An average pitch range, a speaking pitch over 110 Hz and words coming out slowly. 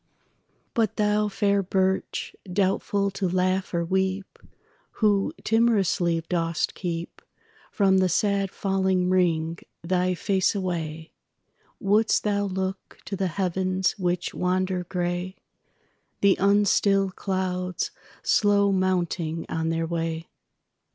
No: narrow, 1.9 semitones; medium, 185 Hz; slow, 95 wpm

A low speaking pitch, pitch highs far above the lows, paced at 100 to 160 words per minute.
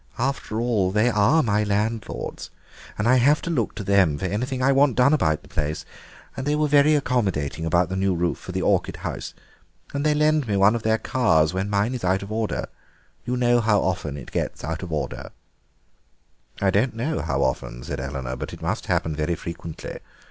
No: low, 105 Hz; wide, 6.6 semitones; fast, 205 wpm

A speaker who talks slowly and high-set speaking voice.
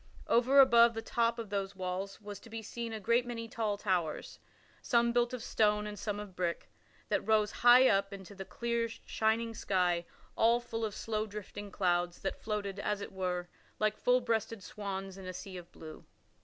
No: average, 195 wpm; high, 210 Hz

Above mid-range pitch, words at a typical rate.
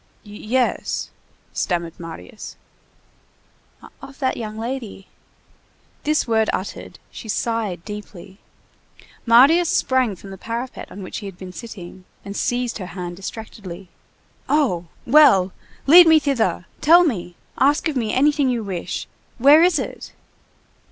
No: high, 225 Hz; slow, 130 wpm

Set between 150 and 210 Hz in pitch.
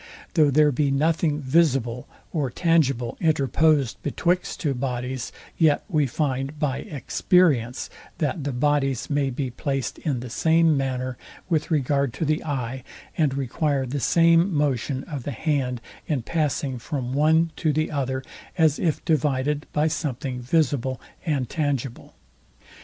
No: medium, 140 Hz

